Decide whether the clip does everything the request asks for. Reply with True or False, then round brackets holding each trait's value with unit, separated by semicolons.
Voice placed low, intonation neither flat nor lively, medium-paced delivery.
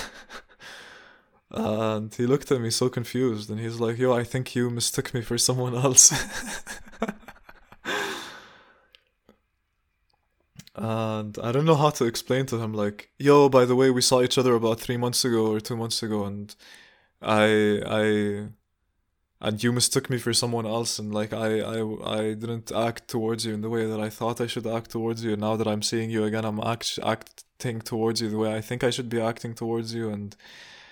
False (115 Hz; 2.3 semitones; 190 wpm)